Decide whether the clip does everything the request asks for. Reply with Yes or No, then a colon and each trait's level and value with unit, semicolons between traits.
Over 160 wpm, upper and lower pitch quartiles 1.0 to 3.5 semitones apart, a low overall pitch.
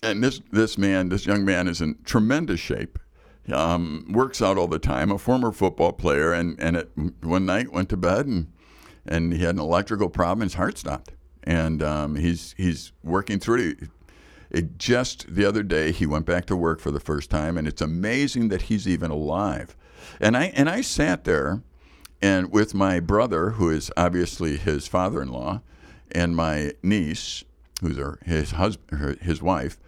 No: average, 185 wpm; average, 4.0 semitones; very low, 85 Hz